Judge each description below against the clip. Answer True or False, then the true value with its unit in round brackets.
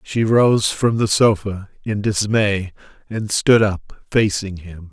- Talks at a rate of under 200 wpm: True (145 wpm)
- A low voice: True (105 Hz)